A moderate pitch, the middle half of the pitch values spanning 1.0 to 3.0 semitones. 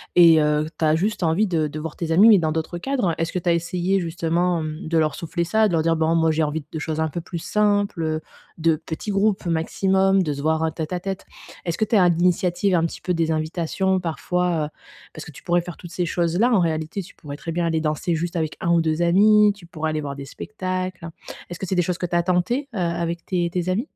Yes: medium, 170 Hz; narrow, 2.4 semitones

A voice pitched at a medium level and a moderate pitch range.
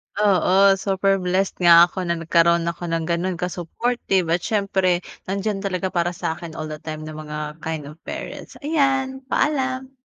Yes: medium, 180 Hz; average, 3.0 semitones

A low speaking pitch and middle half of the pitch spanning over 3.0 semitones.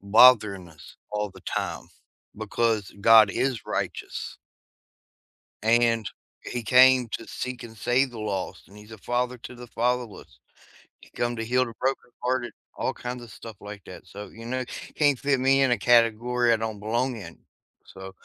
No: low, 115 Hz; average, 2.7 semitones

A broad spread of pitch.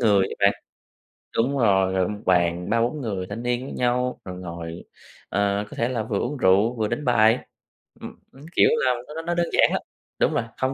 No: average, 4.7 semitones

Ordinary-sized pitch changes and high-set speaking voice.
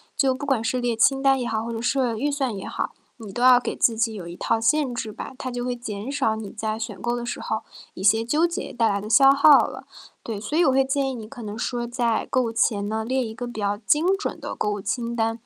Yes: average, 3.3 semitones; high, 235 Hz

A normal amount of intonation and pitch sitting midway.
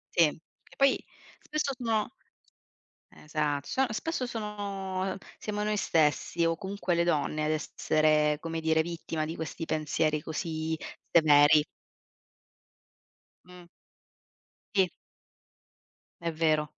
Yes: average, 4.4 semitones; medium, 165 Hz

